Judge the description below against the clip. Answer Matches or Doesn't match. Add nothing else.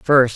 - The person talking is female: Doesn't match